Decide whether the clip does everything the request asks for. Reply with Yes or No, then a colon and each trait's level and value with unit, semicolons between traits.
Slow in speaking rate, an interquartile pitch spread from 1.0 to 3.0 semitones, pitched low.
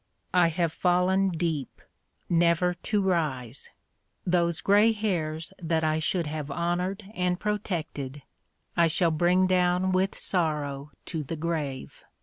No: slow, 130 wpm; average, 2.7 semitones; medium, 170 Hz